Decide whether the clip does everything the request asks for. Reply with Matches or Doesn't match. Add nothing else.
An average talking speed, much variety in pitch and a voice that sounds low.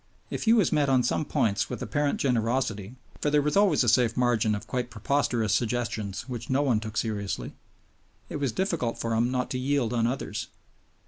Doesn't match